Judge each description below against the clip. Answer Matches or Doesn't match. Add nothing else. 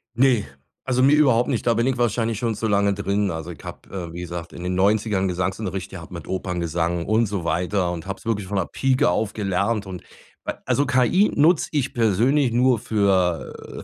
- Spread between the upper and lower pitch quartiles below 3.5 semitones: Doesn't match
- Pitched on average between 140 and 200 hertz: Doesn't match